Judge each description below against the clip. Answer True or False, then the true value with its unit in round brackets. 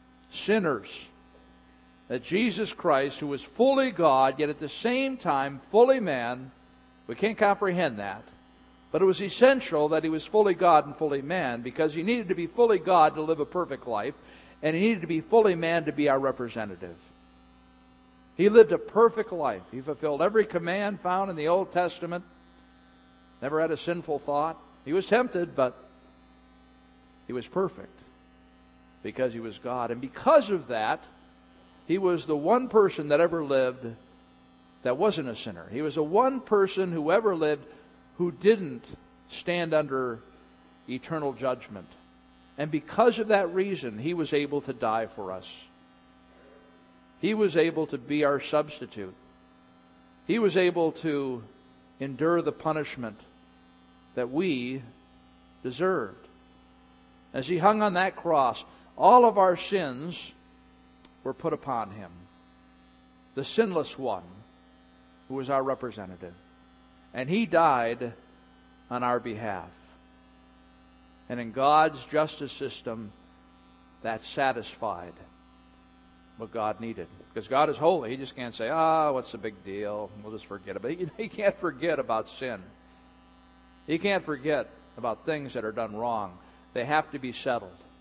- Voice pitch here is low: True (130 Hz)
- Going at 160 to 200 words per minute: False (150 wpm)